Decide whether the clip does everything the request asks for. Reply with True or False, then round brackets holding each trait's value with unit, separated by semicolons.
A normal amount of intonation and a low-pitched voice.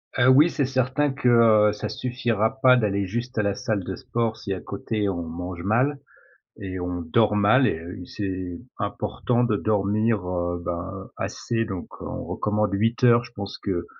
True (3.9 semitones; 105 Hz)